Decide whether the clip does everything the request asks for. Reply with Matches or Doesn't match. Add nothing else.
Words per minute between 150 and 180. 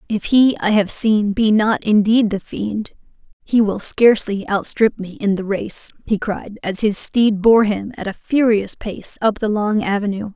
Doesn't match